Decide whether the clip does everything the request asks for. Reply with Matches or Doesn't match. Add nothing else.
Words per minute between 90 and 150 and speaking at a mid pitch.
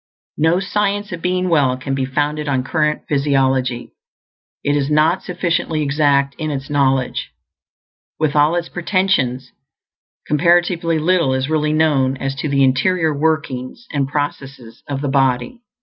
Matches